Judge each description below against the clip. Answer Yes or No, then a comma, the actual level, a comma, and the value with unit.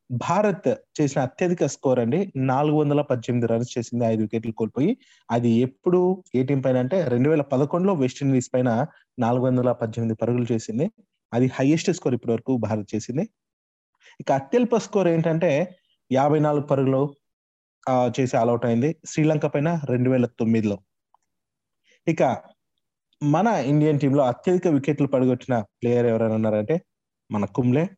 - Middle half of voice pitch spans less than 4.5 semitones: No, average, 5.1 semitones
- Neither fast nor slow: No, fast, 135 wpm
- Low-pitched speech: Yes, low, 130 Hz